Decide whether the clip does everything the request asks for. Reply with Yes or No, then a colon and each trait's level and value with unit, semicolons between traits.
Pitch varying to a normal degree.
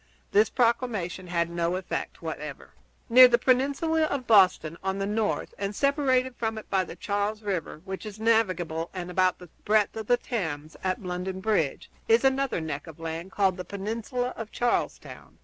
Yes: average, 4.6 semitones